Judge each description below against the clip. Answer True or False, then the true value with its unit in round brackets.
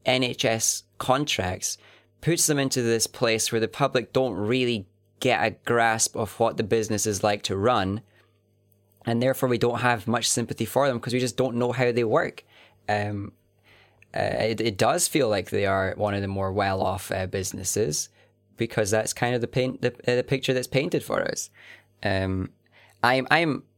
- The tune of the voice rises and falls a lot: False (3.3 semitones)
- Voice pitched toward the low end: True (115 Hz)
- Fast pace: False (185 wpm)